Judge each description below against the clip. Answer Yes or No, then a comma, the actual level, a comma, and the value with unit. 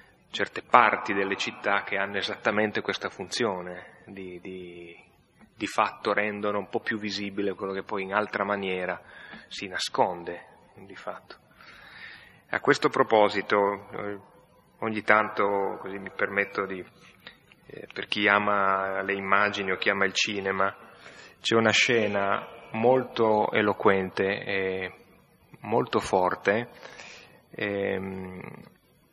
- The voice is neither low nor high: No, low, 100 Hz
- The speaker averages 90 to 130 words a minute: Yes, slow, 115 wpm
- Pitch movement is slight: Yes, narrow, 1.5 semitones